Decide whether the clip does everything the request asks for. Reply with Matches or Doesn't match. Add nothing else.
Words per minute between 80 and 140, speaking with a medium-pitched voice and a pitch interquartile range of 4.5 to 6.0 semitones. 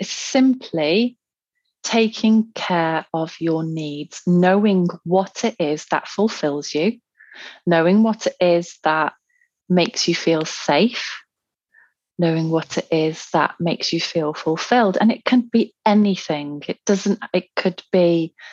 Matches